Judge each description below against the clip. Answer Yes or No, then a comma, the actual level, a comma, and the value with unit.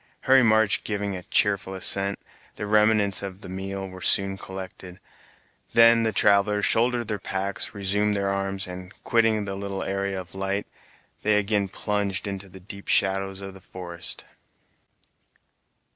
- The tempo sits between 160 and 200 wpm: No, average, 150 wpm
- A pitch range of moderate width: No, narrow, 1.4 semitones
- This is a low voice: Yes, low, 100 Hz